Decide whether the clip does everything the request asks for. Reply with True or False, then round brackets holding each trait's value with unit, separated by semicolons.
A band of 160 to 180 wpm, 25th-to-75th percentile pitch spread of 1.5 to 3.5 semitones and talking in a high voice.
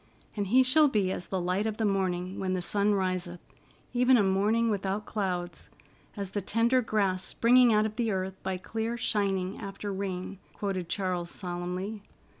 True (175 wpm; 2.8 semitones; 195 Hz)